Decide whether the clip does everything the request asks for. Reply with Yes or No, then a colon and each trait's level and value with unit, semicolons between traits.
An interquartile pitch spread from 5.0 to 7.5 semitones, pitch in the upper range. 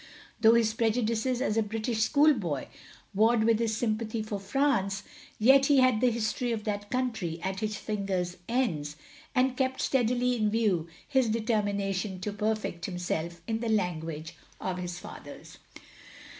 No: average, 3.7 semitones; high, 215 Hz